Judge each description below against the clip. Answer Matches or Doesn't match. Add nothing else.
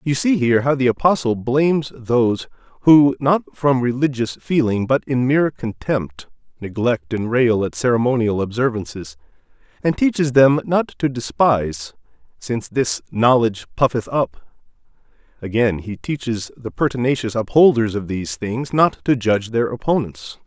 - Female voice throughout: Doesn't match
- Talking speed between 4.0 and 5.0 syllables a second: Matches